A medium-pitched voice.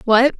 No: high, 245 Hz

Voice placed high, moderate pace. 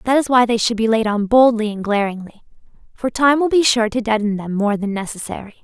No: high, 225 Hz; fast, 235 wpm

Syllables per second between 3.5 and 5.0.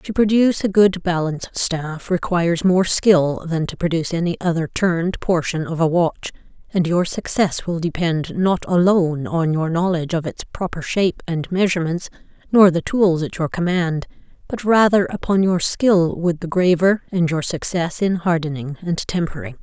Yes: 4.9 syllables/s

